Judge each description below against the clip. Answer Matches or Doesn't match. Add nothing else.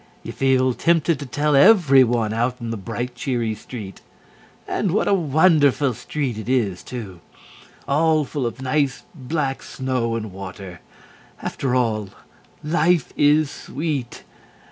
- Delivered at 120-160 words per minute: Matches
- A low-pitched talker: Matches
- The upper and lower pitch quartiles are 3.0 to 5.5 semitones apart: Matches